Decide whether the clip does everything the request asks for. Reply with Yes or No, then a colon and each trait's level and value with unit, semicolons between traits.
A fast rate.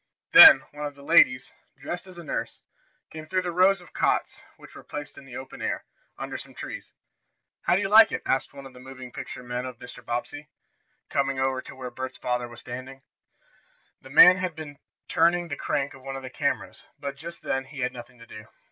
Yes: fast, 220 wpm